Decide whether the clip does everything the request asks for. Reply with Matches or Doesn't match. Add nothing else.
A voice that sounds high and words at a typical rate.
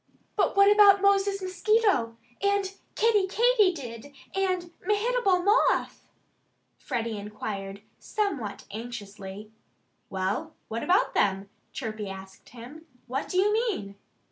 Doesn't match